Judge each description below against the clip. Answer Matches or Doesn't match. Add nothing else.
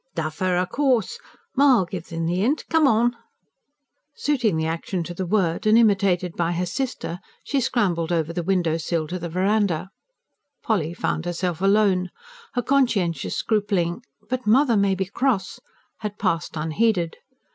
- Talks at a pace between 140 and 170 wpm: Matches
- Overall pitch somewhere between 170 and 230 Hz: Matches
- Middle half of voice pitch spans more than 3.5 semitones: Matches